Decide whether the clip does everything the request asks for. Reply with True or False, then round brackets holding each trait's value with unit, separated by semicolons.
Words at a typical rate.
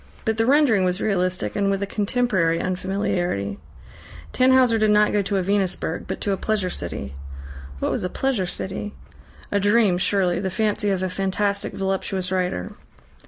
True (165 wpm)